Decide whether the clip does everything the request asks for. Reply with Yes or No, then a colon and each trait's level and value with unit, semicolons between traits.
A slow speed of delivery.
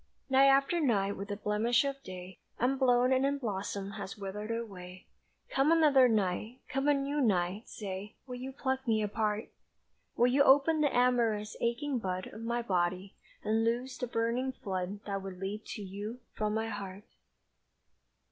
No: average, 165 wpm